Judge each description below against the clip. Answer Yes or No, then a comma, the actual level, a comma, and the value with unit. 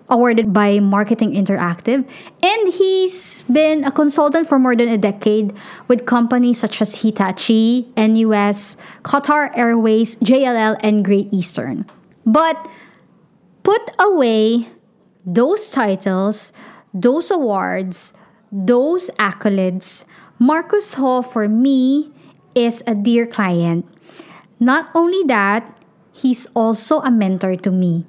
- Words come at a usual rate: No, slow, 110 wpm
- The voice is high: Yes, high, 230 Hz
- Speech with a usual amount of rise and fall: Yes, average, 4.5 semitones